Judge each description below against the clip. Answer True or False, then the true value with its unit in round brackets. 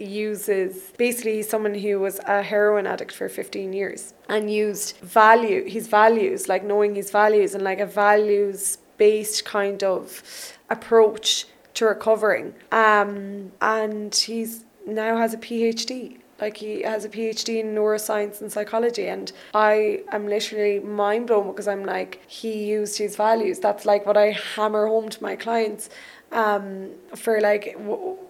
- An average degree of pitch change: False (1.3 semitones)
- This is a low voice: False (210 Hz)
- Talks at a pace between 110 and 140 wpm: False (155 wpm)